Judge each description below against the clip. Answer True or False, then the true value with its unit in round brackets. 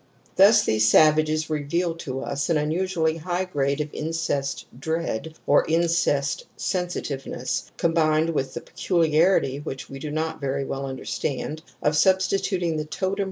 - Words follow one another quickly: False (145 wpm)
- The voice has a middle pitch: True (155 Hz)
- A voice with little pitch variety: False (3.3 semitones)